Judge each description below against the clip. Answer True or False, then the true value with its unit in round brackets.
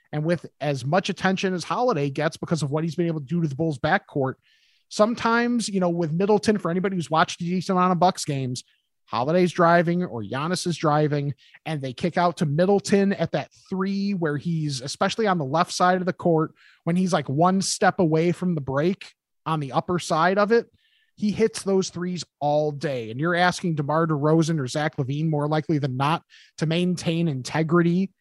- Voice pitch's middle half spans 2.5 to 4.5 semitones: True (3.0 semitones)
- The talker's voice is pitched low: False (170 Hz)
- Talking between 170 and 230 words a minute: True (205 wpm)